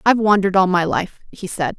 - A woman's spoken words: Yes, female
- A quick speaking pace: Yes, fast, 235 wpm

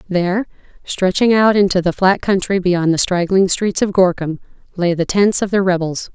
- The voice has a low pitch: No, medium, 185 Hz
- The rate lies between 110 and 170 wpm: No, average, 185 wpm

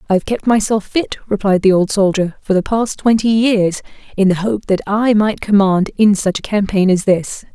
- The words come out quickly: Yes, fast, 215 wpm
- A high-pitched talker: Yes, high, 205 Hz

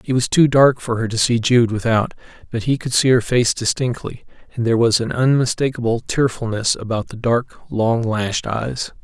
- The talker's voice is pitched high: No, low, 120 Hz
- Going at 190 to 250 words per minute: Yes, average, 195 wpm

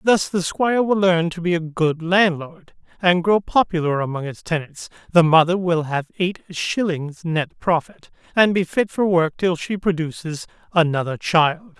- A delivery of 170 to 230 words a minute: Yes, average, 175 wpm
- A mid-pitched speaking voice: Yes, medium, 170 Hz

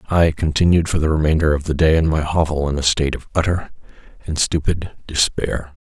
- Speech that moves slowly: No, average, 195 wpm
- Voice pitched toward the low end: Yes, very low, 80 Hz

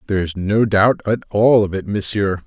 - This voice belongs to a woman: No, male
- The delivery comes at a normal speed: No, fast, 220 wpm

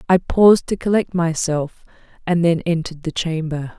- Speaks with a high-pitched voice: No, medium, 170 Hz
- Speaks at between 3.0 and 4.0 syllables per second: No, 5.1 syllables/s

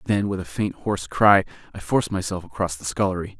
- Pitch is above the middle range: No, very low, 95 Hz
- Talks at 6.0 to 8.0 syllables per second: Yes, 6.1 syllables/s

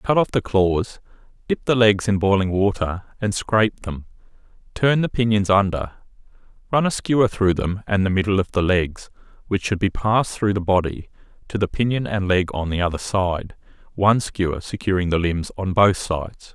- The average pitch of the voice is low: Yes, low, 100 Hz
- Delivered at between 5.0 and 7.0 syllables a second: Yes, 5.1 syllables/s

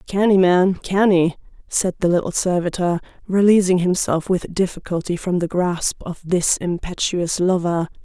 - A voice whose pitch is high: No, medium, 180 Hz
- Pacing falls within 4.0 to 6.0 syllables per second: Yes, 4.5 syllables/s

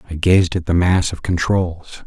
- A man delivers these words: Yes, male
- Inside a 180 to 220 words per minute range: Yes, fast, 205 wpm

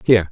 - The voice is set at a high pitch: No, low, 100 Hz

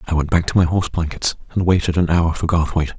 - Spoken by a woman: No, male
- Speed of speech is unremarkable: No, fast, 260 wpm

